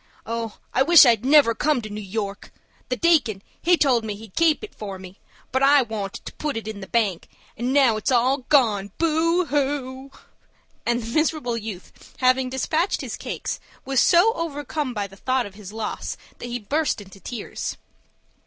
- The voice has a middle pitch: No, high, 245 Hz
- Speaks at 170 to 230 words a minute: Yes, average, 185 wpm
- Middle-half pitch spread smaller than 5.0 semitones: No, average, 5.3 semitones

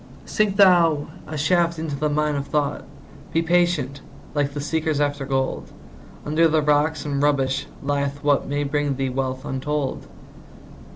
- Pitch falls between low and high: Yes, medium, 145 Hz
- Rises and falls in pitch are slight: Yes, narrow, 2.0 semitones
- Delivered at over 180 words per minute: No, average, 155 wpm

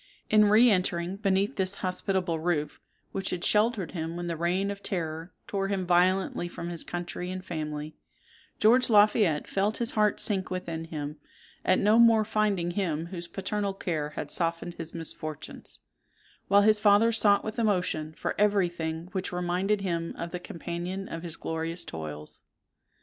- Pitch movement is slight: No, average, 3.3 semitones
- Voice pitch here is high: No, medium, 180 Hz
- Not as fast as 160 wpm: No, average, 165 wpm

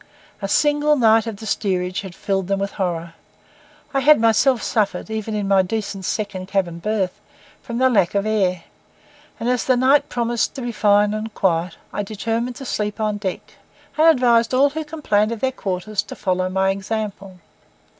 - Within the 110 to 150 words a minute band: No, average, 185 wpm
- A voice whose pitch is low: No, high, 215 Hz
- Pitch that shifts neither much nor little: Yes, average, 3.7 semitones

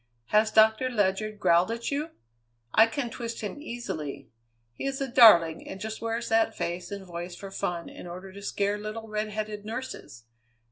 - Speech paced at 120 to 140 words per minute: No, average, 175 wpm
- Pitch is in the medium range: No, high, 215 Hz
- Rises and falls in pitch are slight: No, average, 3.2 semitones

